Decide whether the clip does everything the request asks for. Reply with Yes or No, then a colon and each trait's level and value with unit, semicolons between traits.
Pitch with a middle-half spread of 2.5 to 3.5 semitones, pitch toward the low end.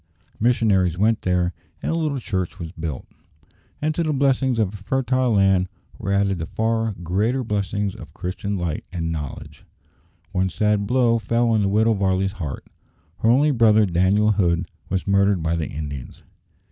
No: average, 4.1 semitones; low, 100 Hz